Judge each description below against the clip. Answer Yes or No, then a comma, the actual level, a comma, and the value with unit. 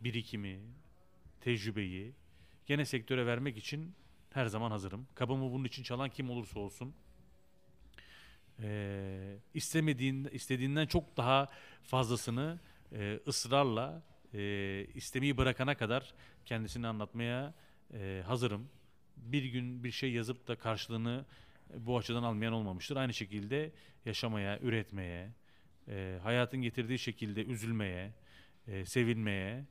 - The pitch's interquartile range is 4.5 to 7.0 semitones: No, average, 4.0 semitones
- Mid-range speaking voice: No, low, 120 Hz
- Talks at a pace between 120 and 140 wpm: No, average, 110 wpm